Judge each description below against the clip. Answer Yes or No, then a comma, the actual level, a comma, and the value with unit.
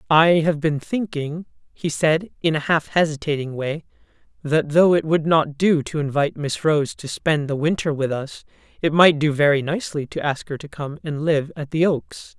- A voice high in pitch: No, medium, 155 Hz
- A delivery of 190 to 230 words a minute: Yes, fast, 205 wpm